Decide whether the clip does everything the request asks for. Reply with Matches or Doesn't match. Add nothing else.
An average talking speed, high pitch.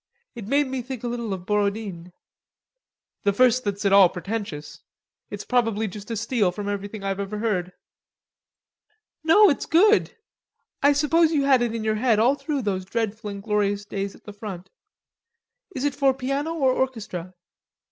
Matches